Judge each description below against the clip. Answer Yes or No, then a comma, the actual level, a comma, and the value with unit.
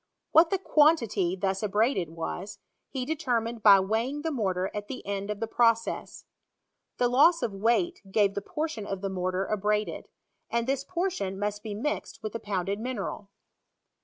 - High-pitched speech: Yes, high, 215 Hz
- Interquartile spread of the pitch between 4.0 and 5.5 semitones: Yes, average, 4.8 semitones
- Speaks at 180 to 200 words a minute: No, average, 165 wpm